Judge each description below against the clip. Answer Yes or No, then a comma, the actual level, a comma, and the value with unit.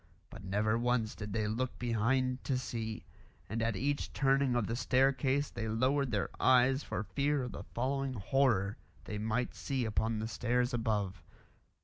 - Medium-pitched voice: No, low, 120 Hz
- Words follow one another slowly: No, average, 165 wpm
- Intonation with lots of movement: No, average, 3.3 semitones